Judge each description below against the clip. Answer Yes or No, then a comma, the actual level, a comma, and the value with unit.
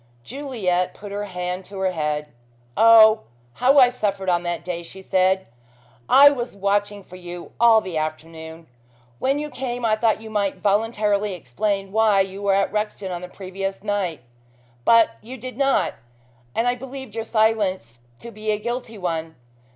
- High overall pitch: Yes, high, 200 Hz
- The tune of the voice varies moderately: Yes, average, 3.7 semitones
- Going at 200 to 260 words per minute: No, average, 170 wpm